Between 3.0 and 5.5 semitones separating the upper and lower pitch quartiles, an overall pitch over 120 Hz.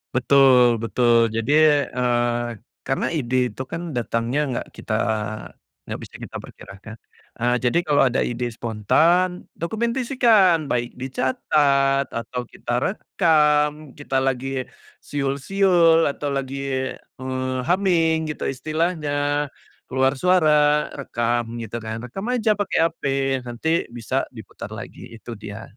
Yes: average, 4.9 semitones; low, 135 Hz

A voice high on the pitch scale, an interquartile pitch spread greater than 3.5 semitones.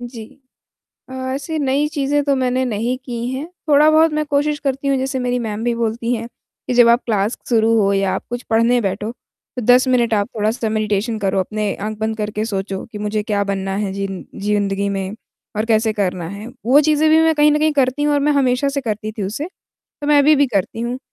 Yes: high, 235 Hz; average, 4.7 semitones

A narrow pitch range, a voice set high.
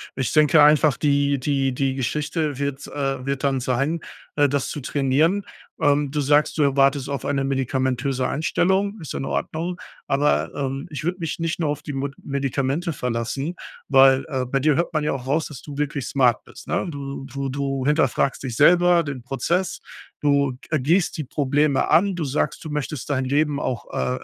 No: narrow, 2.2 semitones; medium, 140 Hz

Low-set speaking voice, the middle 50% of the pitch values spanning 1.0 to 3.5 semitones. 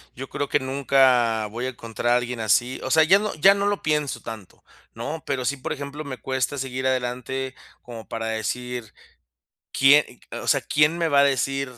Yes: low, 130 Hz; average, 2.7 semitones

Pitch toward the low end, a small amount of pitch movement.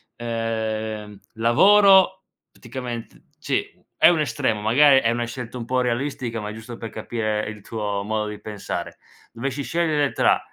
No: low, 115 Hz; average, 3.3 semitones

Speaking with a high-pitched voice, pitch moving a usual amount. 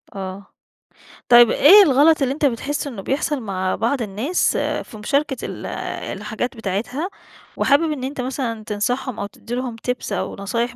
Yes: high, 245 Hz; average, 4.9 semitones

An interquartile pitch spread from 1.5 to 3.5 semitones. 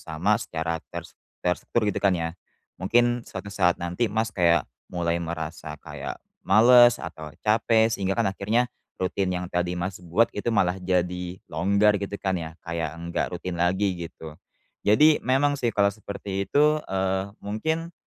No: average, 4.0 semitones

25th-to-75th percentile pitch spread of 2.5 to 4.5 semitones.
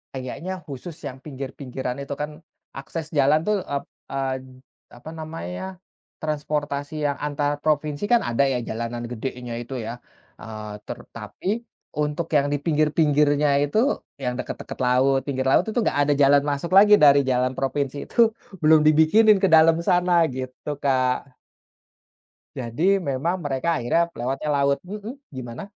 Yes: average, 3.4 semitones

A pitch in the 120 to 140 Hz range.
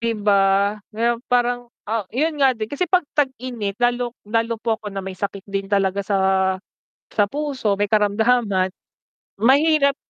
No: high, 230 Hz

